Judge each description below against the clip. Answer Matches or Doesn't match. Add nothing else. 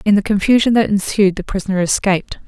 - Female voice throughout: Matches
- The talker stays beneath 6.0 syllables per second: Doesn't match